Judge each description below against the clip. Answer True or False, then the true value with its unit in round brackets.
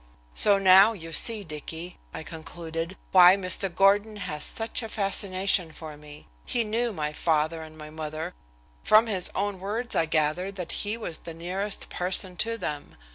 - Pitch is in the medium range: True (180 Hz)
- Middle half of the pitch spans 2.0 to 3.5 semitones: False (4.2 semitones)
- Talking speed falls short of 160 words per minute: False (170 wpm)